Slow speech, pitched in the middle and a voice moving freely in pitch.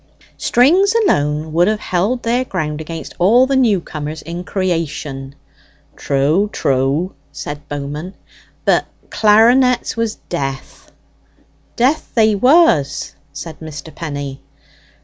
Yes: slow, 110 wpm; medium, 170 Hz; wide, 7.7 semitones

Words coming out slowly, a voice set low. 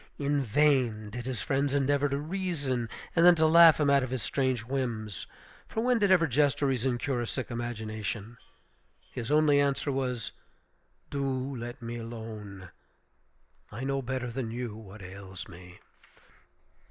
No: average, 160 wpm; low, 130 Hz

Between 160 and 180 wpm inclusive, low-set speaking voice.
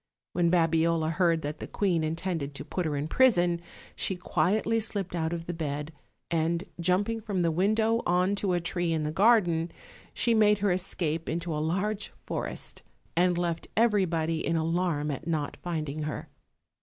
No: average, 170 wpm; medium, 170 Hz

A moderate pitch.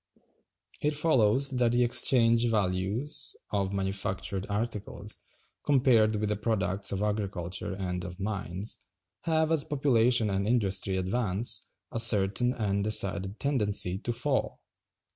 No: low, 105 Hz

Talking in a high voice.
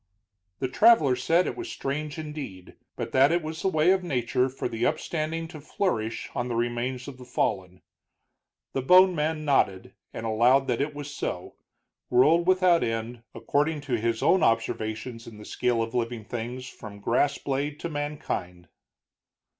No: low, 130 Hz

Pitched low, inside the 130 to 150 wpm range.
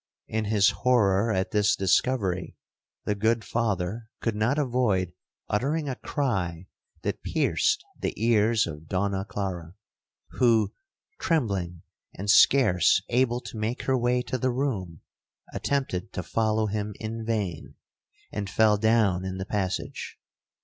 Yes: low, 110 Hz; slow, 135 wpm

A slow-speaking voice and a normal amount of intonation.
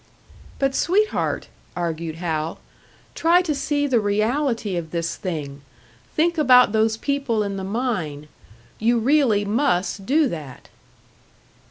No: slow, 125 wpm; wide, 8.3 semitones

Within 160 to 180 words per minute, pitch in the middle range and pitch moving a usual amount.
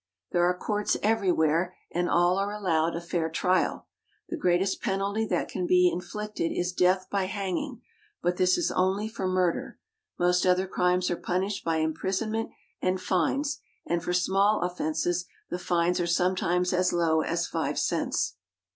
No: average, 165 wpm; medium, 180 Hz; narrow, 1.8 semitones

